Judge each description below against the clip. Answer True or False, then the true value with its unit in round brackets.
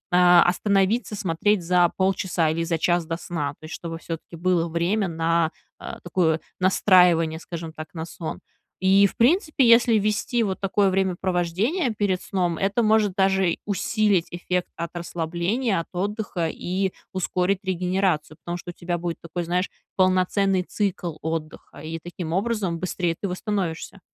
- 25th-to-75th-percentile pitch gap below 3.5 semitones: True (2.8 semitones)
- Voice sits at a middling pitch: True (180 Hz)